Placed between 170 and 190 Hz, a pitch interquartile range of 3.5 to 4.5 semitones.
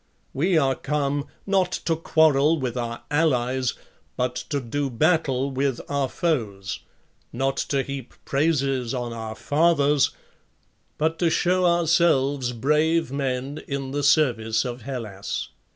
No: medium, 140 Hz; average, 3.8 semitones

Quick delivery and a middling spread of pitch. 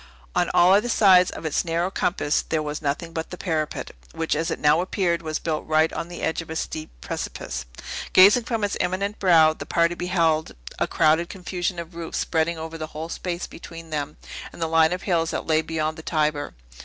No: fast, 210 wpm; narrow, 2.1 semitones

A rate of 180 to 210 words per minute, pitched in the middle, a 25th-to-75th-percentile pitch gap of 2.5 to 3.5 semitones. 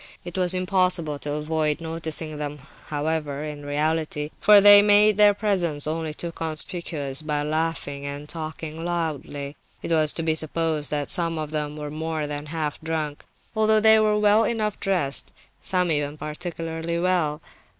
No: average, 160 wpm; medium, 160 Hz; average, 2.9 semitones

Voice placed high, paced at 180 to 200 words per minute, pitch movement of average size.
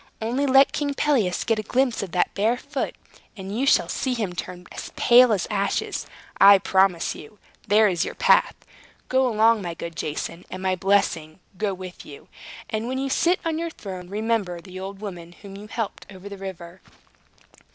Yes: high, 200 Hz; average, 190 wpm; average, 4.5 semitones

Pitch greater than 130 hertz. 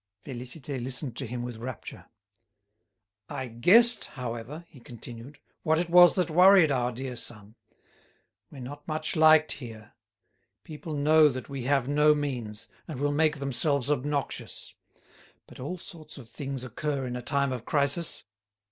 Yes: medium, 140 Hz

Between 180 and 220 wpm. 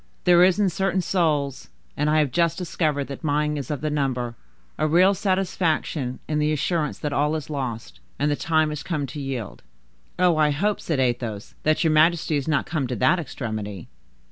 Yes: average, 190 wpm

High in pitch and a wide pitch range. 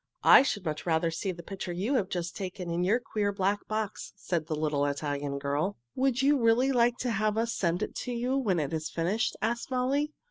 Yes: high, 195 Hz; wide, 6.1 semitones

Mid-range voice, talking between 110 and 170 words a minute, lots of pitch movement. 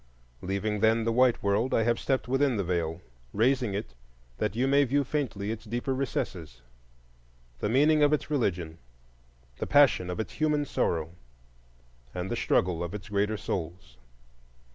No: low, 105 Hz; average, 155 wpm; wide, 7.0 semitones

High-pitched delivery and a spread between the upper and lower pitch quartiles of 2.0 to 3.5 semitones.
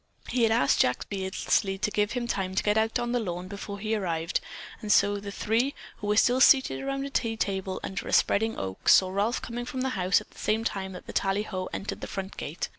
Yes: high, 205 Hz; average, 3.2 semitones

